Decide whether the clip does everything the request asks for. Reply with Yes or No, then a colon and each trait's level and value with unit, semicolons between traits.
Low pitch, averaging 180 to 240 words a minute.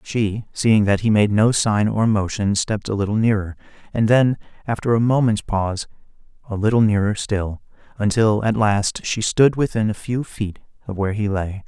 Yes: low, 105 Hz; average, 185 wpm